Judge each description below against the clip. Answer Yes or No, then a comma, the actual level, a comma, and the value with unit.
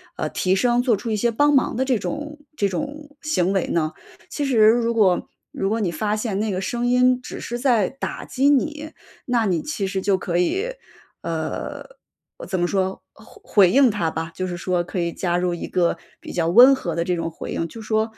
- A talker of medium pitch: No, high, 215 Hz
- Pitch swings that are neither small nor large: No, wide, 5.8 semitones